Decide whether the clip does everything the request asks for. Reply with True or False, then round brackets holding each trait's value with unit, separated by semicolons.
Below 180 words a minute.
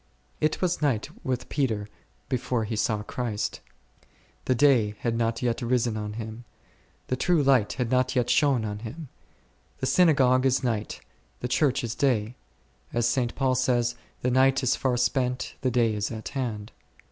True (170 wpm)